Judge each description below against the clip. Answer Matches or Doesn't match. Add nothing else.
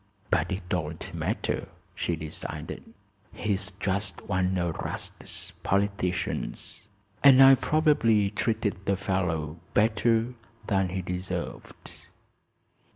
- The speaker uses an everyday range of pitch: Matches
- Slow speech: Matches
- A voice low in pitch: Matches